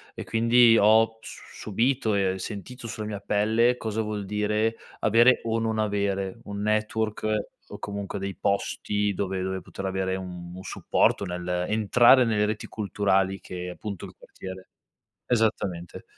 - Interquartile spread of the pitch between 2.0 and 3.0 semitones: Yes, narrow, 2.6 semitones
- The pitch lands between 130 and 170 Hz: No, low, 105 Hz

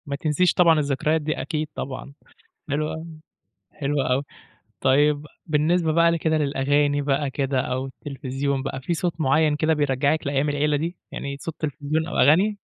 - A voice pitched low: No, medium, 145 Hz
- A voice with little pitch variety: Yes, narrow, 2.2 semitones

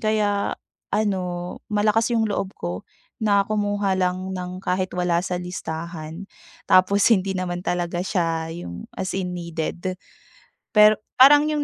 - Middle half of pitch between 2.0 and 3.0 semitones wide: Yes, narrow, 2.6 semitones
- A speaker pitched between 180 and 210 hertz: Yes, medium, 185 Hz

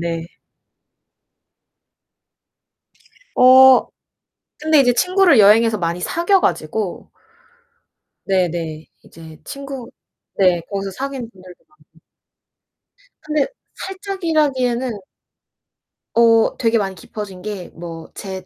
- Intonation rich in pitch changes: Yes, wide, 7.1 semitones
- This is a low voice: No, high, 225 Hz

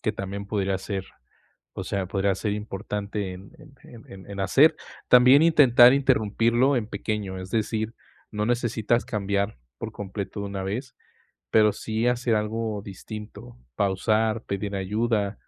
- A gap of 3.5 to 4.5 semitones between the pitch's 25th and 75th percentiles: No, average, 2.7 semitones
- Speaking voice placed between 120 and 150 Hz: No, low, 105 Hz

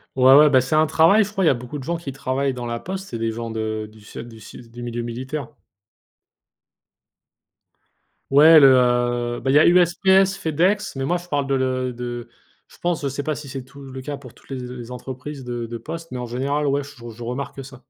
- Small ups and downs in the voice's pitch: No, average, 3.7 semitones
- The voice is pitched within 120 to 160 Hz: Yes, low, 135 Hz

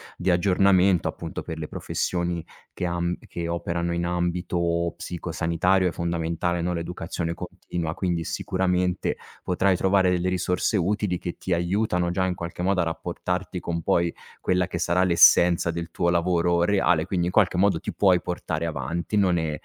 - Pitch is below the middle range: Yes, very low, 90 Hz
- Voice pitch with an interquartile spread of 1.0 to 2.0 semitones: Yes, narrow, 1.3 semitones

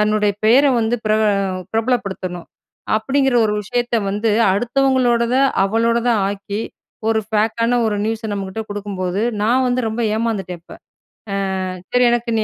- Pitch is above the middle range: Yes, high, 220 Hz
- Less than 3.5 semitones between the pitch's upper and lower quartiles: Yes, average, 2.7 semitones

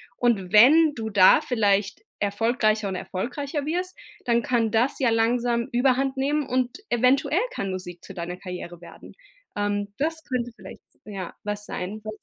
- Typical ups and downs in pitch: Yes, average, 4.3 semitones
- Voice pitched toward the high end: Yes, high, 230 Hz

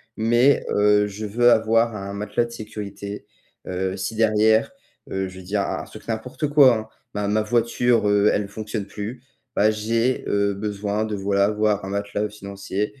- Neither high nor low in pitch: No, low, 105 Hz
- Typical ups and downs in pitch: No, narrow, 1.8 semitones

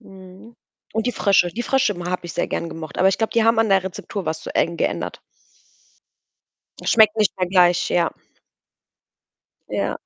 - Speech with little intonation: No, average, 3.7 semitones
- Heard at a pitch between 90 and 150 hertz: No, high, 190 Hz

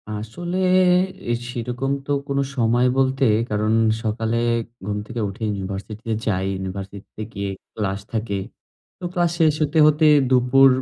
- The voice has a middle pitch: No, low, 115 Hz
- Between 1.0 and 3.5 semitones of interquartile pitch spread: No, average, 4.8 semitones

